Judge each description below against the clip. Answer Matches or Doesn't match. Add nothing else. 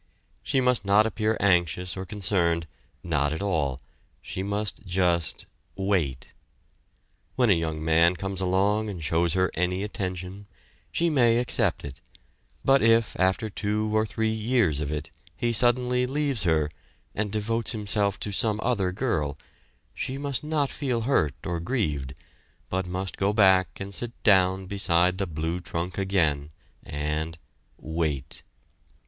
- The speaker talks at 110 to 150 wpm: Matches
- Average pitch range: Matches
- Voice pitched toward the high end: Doesn't match